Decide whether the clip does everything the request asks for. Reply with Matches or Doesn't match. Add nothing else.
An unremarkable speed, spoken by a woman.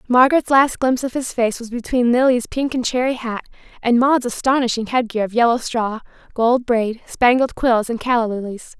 Matches